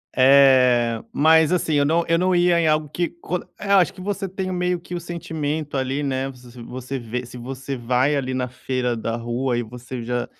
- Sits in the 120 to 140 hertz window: Yes, low, 135 Hz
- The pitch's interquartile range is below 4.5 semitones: No, average, 5.1 semitones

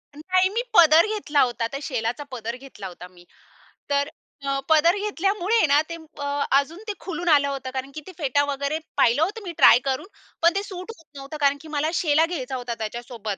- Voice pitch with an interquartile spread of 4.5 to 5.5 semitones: Yes, average, 4.8 semitones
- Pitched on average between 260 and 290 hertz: Yes, very high, 285 Hz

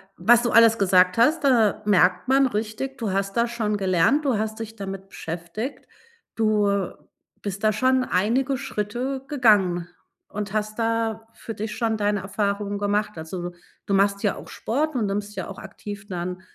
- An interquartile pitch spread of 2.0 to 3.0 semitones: Yes, average, 2.7 semitones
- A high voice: Yes, high, 210 Hz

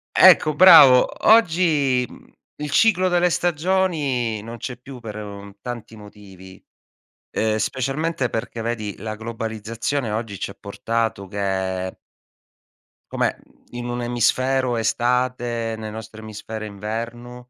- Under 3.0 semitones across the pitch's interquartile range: No, average, 3.8 semitones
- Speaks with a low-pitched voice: Yes, low, 120 Hz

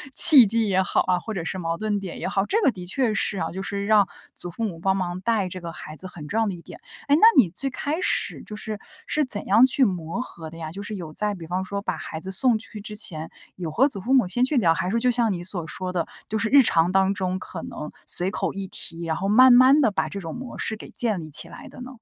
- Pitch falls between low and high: No, high, 195 Hz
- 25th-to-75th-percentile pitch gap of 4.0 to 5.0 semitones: Yes, average, 4.4 semitones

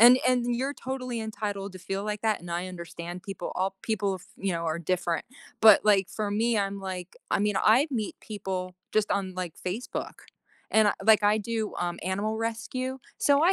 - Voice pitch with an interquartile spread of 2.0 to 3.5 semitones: Yes, average, 3.2 semitones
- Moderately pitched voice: No, high, 205 Hz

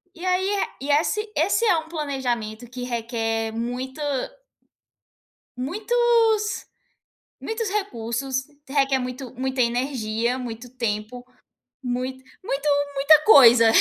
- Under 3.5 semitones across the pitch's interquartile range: No, average, 5.2 semitones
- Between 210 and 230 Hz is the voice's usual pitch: No, very high, 260 Hz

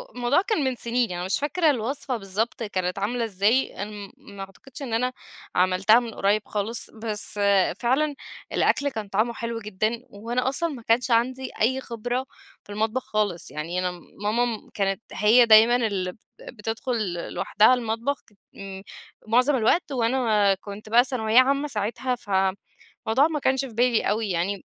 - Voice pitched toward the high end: Yes, high, 225 Hz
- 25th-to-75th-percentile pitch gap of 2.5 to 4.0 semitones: Yes, average, 3.6 semitones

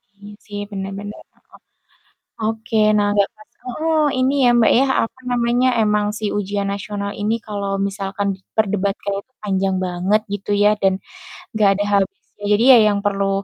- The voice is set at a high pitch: Yes, high, 205 Hz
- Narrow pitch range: Yes, narrow, 1.8 semitones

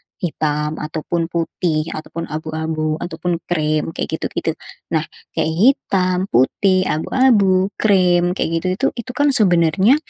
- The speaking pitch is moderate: Yes, medium, 170 Hz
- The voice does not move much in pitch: No, average, 3.0 semitones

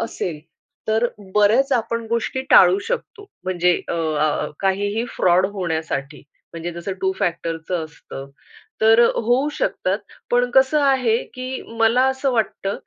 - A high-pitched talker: Yes, high, 215 Hz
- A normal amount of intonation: No, wide, 6.2 semitones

